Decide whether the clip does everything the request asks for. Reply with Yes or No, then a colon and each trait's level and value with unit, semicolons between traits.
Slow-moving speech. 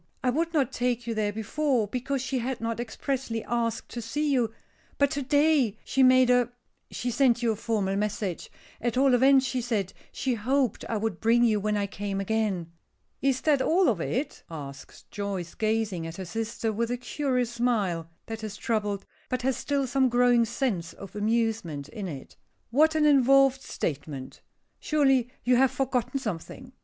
No: average, 180 wpm